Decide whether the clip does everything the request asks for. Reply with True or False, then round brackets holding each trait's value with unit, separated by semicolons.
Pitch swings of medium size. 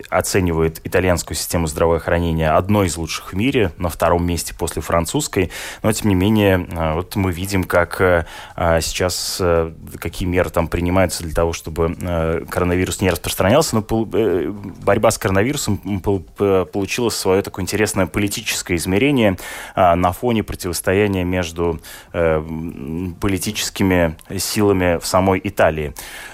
True (3.1 semitones)